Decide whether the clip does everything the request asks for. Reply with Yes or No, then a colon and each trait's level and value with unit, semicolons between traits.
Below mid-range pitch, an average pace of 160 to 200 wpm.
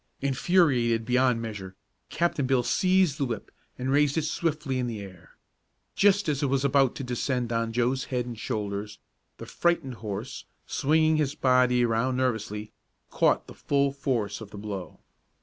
Yes: low, 125 Hz; average, 165 wpm